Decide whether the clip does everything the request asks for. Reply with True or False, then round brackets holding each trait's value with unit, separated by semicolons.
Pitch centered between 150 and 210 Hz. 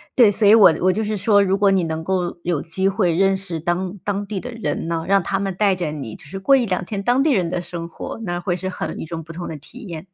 True (190 Hz)